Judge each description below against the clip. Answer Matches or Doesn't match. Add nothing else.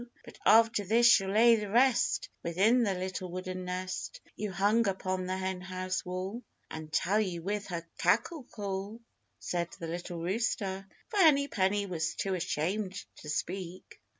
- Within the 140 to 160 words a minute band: Matches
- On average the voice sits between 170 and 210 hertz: Matches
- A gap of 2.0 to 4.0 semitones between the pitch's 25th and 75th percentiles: Matches